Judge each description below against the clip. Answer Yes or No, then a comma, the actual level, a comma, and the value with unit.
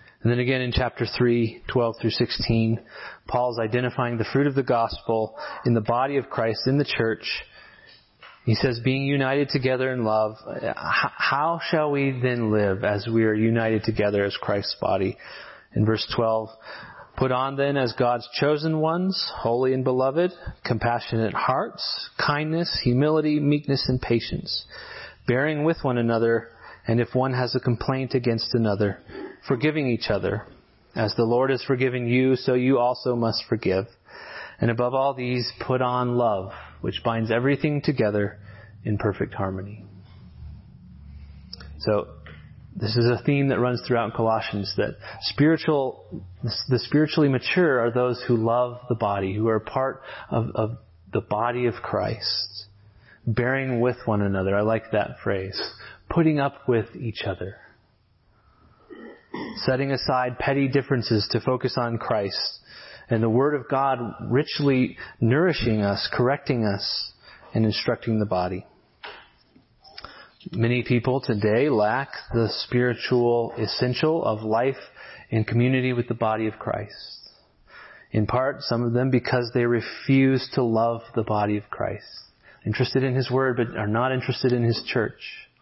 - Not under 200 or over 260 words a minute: No, average, 145 wpm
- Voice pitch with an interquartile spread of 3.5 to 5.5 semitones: No, average, 3.0 semitones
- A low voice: Yes, low, 120 Hz